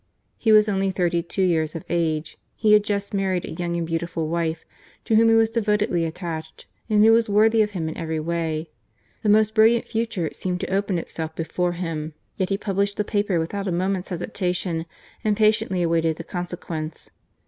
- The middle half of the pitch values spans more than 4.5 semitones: No, average, 4.1 semitones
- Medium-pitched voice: Yes, medium, 180 Hz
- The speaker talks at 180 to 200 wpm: Yes, average, 190 wpm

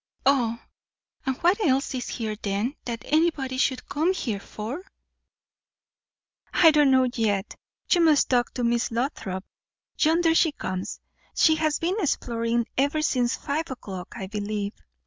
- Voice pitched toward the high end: Yes, very high, 260 Hz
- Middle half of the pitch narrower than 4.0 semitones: No, wide, 5.4 semitones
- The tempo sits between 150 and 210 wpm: No, average, 140 wpm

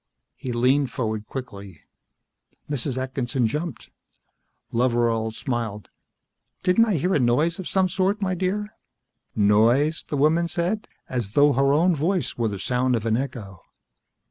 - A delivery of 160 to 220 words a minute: No, average, 145 wpm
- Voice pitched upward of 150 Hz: No, low, 130 Hz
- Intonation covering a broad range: Yes, wide, 6.4 semitones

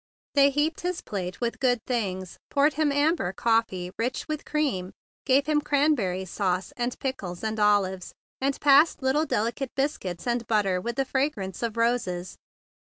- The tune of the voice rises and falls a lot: Yes, wide, 6.7 semitones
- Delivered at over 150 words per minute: Yes, average, 160 wpm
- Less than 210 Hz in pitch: No, high, 235 Hz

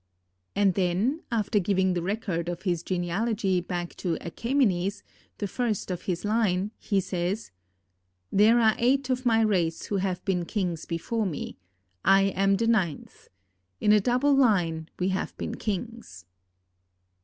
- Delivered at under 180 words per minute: Yes, average, 150 wpm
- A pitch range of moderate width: Yes, average, 4.0 semitones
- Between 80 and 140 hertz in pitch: No, high, 195 Hz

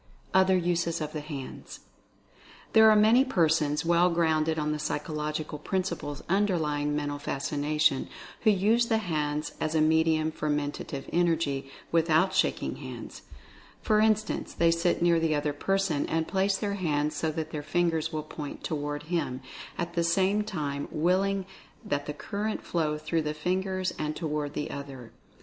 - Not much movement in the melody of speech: No, average, 3.6 semitones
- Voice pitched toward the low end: No, medium, 160 Hz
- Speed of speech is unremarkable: Yes, average, 160 wpm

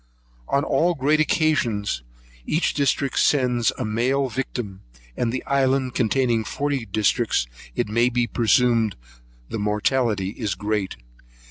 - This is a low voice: Yes, low, 120 Hz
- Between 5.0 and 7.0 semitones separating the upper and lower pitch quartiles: No, average, 3.8 semitones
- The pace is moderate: No, slow, 125 wpm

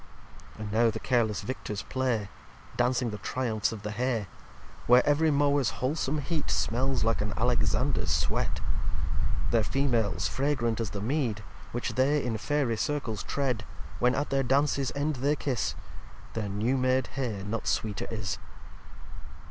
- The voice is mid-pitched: No, low, 125 Hz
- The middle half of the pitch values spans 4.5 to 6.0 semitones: No, average, 3.9 semitones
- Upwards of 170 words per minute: No, average, 150 wpm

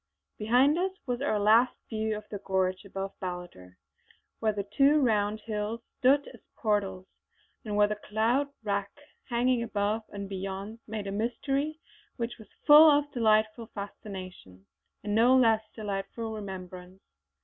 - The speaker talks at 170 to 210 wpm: No, average, 145 wpm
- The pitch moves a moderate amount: Yes, average, 3.2 semitones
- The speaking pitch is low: No, high, 215 Hz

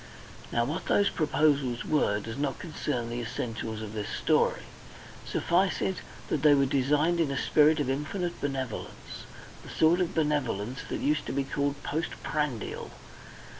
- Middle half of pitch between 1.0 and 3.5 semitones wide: No, average, 3.9 semitones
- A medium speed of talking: Yes, average, 160 wpm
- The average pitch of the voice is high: No, medium, 145 Hz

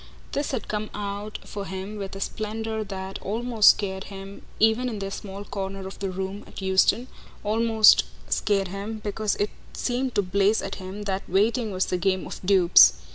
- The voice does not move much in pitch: Yes, narrow, 2.1 semitones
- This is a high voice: Yes, high, 200 Hz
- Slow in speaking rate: No, average, 185 wpm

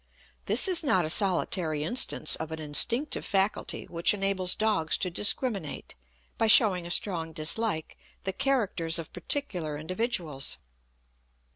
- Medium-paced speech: No, slow, 130 wpm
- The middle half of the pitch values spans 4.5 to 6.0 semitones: Yes, wide, 5.4 semitones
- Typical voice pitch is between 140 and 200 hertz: Yes, medium, 185 Hz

